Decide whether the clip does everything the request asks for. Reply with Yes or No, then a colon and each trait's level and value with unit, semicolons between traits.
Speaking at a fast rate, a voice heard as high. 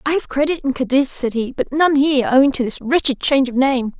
Yes: fast, 255 wpm; very high, 270 Hz